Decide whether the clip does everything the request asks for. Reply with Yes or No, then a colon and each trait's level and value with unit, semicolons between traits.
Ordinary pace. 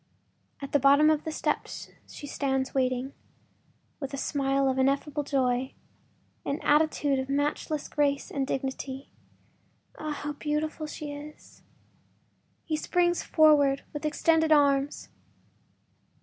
No: slow, 120 wpm